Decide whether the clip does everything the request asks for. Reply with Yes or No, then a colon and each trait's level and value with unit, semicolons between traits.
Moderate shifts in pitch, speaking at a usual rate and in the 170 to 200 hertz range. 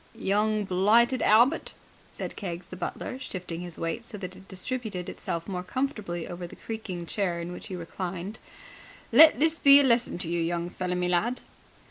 Yes: average, 4.8 semitones; average, 180 wpm; medium, 185 Hz